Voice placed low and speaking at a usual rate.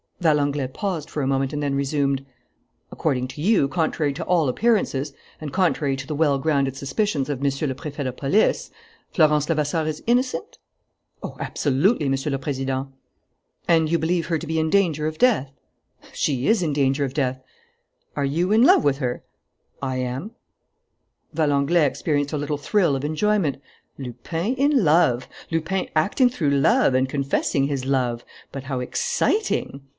No: medium, 145 Hz; average, 165 wpm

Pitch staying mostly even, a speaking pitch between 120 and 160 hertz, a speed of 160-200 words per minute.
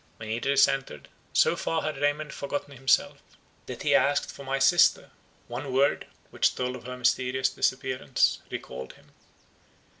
No: narrow, 2.0 semitones; low, 135 Hz; average, 150 wpm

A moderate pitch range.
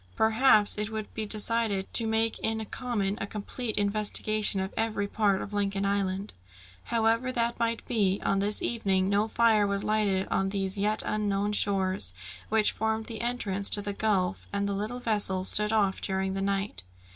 No: narrow, 1.9 semitones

